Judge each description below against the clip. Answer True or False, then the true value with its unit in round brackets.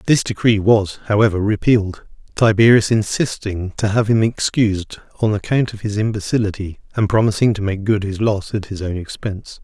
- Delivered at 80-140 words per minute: False (170 wpm)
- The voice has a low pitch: True (105 Hz)